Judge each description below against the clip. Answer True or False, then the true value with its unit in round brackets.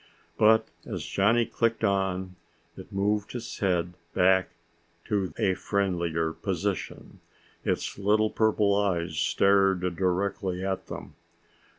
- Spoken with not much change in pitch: True (2.2 semitones)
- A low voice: True (95 Hz)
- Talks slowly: True (110 wpm)